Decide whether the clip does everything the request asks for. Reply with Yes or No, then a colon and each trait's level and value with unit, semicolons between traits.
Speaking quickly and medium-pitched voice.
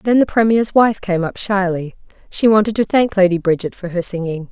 No: fast, 215 wpm; high, 195 Hz